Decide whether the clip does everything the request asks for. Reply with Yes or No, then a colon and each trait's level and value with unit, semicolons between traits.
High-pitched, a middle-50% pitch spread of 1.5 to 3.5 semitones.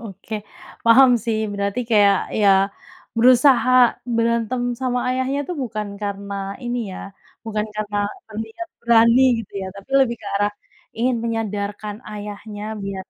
Yes: high, 225 Hz; average, 2.9 semitones